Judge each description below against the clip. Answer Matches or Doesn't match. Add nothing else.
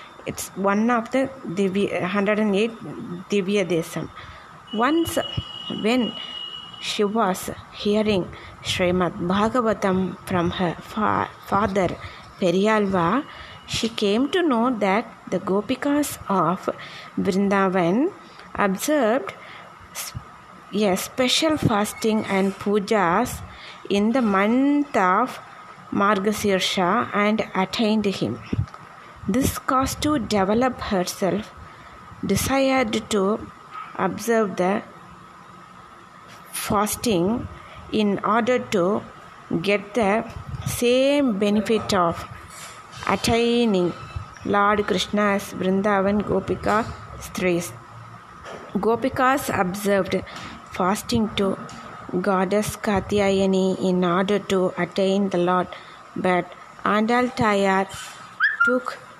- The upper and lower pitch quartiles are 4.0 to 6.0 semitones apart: Doesn't match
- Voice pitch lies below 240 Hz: Matches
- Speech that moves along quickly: Doesn't match